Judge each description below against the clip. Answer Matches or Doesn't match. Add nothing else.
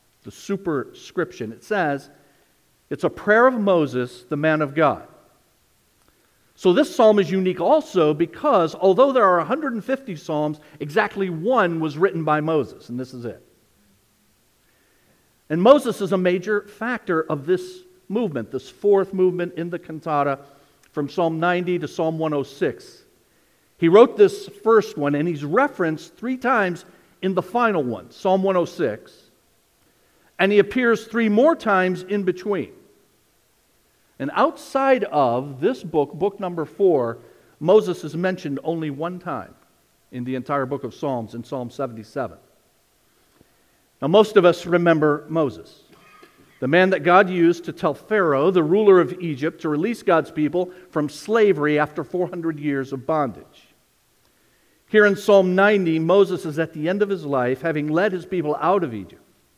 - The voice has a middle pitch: Matches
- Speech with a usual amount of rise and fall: Matches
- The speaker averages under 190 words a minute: Matches